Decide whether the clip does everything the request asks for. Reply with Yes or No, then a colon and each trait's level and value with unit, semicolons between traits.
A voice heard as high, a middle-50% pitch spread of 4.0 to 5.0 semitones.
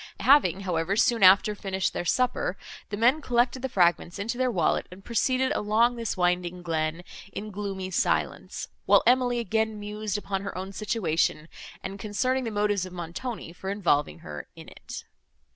Yes: high, 200 Hz; average, 4.3 semitones